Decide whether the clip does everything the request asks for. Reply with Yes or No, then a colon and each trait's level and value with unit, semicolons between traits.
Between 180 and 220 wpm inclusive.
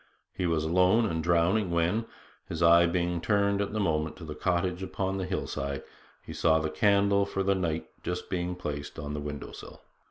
Yes: average, 195 wpm